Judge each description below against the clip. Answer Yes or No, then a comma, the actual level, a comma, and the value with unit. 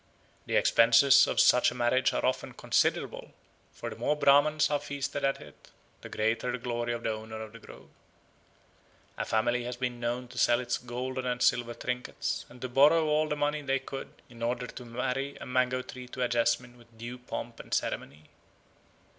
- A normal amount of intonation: No, narrow, 2.2 semitones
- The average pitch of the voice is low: Yes, low, 125 Hz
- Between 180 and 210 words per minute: Yes, average, 195 wpm